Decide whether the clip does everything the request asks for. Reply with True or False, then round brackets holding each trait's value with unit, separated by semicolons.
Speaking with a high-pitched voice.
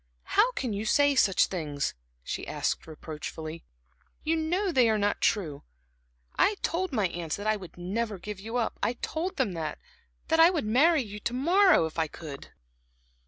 True (215 Hz)